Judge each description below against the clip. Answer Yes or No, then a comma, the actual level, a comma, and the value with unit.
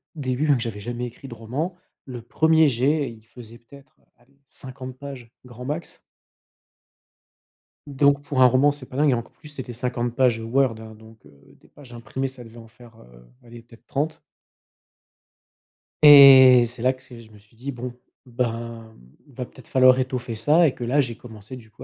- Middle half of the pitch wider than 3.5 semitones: No, average, 2.9 semitones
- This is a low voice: Yes, low, 125 Hz